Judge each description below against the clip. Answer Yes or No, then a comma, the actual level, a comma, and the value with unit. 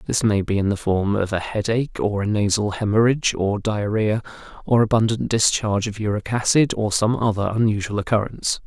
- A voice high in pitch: No, low, 105 Hz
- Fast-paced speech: No, average, 180 wpm